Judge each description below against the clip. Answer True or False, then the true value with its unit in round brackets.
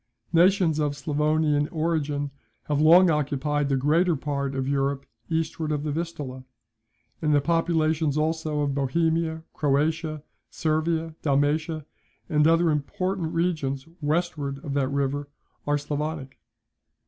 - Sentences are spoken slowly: True (125 wpm)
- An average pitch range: False (2.2 semitones)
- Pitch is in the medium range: True (150 Hz)